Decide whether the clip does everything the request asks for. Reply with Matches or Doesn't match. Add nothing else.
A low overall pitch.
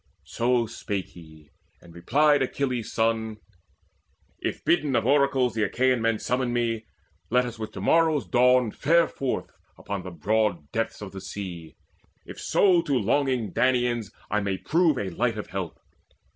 Matches